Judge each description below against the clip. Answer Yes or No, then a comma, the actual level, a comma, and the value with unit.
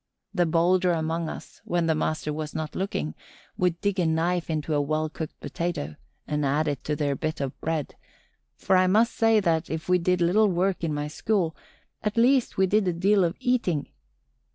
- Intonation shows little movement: No, average, 3.2 semitones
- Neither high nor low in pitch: Yes, medium, 170 Hz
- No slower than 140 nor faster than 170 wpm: No, average, 200 wpm